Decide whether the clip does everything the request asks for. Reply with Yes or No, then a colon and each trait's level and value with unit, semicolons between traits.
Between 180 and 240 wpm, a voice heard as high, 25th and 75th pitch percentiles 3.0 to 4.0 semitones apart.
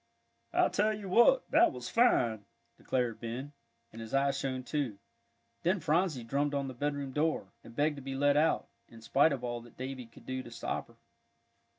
No: average, 195 wpm; low, 135 Hz; average, 3.5 semitones